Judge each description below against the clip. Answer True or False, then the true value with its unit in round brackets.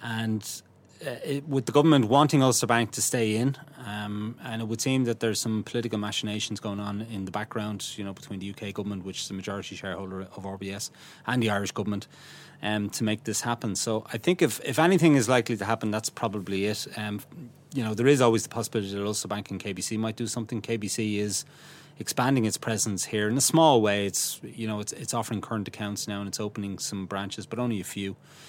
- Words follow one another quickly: True (220 wpm)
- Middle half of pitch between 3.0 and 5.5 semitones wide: False (2.6 semitones)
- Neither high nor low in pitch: False (110 Hz)